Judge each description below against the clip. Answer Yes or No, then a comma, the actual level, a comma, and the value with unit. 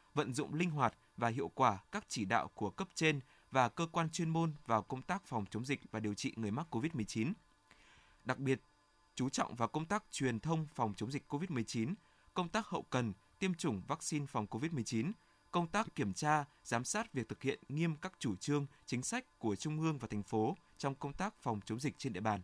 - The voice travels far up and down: Yes, wide, 5.7 semitones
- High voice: No, medium, 140 Hz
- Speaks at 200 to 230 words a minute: Yes, average, 220 wpm